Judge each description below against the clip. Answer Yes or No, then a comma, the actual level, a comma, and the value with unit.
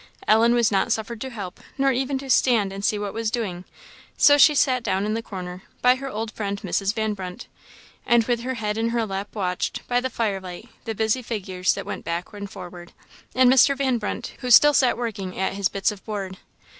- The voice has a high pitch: Yes, high, 220 Hz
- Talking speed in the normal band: No, fast, 220 wpm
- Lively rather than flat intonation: No, average, 3.9 semitones